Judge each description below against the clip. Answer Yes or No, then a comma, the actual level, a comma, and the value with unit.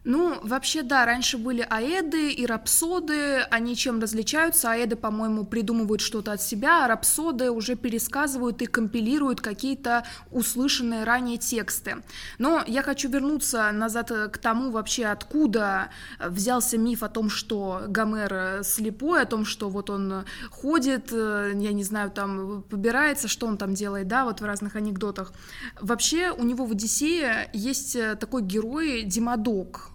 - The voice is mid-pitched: No, high, 230 Hz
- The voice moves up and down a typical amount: Yes, average, 3.6 semitones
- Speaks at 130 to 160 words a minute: Yes, average, 145 wpm